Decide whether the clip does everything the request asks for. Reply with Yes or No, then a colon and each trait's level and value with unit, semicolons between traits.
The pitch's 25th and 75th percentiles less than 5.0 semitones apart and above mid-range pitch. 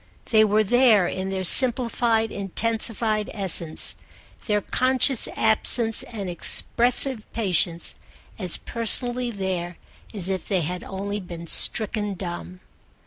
Yes: average, 3.7 semitones; high, 210 Hz